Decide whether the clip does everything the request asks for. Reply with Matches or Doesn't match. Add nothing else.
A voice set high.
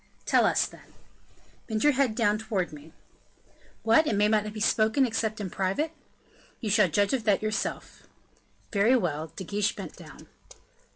Matches